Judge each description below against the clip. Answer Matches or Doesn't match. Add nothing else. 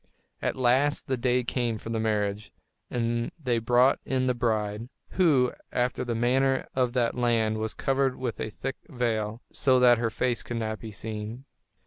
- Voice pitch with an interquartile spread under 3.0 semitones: Matches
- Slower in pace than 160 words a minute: Doesn't match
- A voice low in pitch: Matches